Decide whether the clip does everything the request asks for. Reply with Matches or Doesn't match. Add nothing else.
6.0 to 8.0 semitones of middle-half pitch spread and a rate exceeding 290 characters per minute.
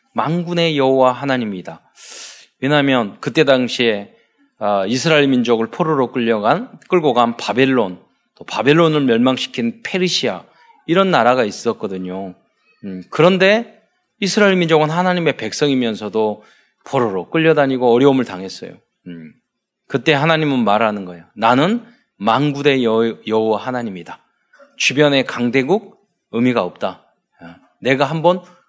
Matches